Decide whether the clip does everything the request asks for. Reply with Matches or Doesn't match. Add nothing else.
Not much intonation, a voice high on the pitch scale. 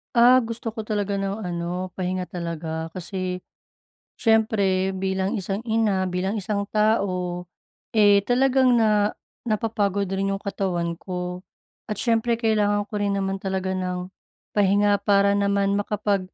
Matches